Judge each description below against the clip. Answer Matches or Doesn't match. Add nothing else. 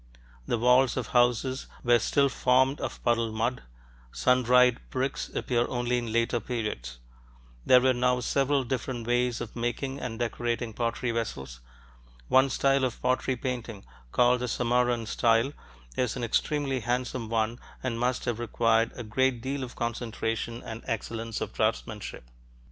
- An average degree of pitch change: Doesn't match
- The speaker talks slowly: Doesn't match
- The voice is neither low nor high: Doesn't match